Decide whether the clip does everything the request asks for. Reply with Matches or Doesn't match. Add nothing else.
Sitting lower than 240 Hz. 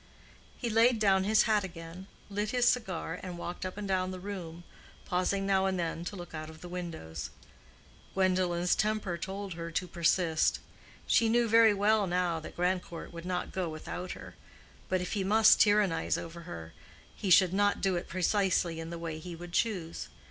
Matches